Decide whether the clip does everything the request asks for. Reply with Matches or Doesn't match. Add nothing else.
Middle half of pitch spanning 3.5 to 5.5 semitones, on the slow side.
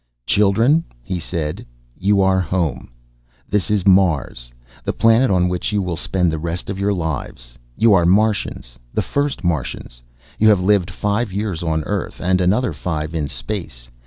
Doesn't match